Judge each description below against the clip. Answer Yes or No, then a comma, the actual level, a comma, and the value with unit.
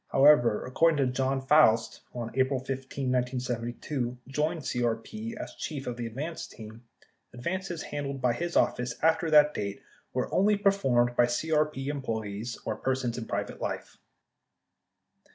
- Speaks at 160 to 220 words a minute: No, average, 145 wpm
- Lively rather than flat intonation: No, average, 3.9 semitones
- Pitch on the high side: No, low, 130 Hz